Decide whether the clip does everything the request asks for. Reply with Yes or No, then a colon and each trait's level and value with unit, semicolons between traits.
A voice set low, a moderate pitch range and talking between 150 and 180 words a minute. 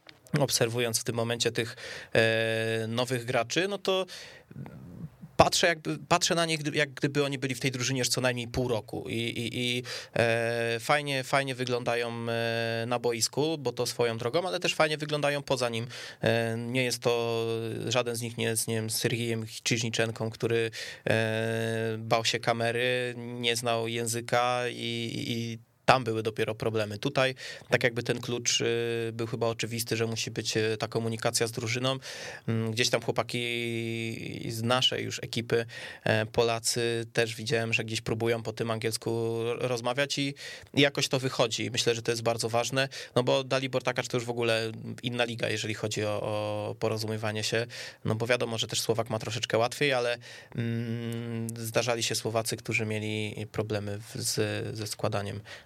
No: low, 115 Hz; narrow, 1.7 semitones; fast, 160 wpm